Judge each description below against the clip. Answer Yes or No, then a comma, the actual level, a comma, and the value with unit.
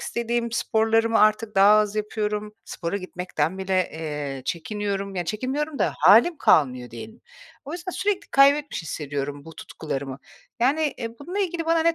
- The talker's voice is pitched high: Yes, high, 210 Hz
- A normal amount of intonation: No, wide, 8.6 semitones